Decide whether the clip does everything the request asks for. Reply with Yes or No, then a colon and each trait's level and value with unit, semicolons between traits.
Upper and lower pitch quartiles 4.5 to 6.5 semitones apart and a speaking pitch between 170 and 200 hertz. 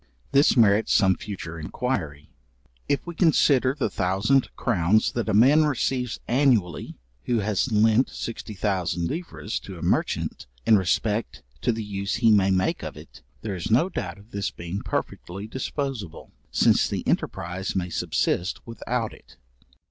No: average, 4.9 semitones; low, 105 Hz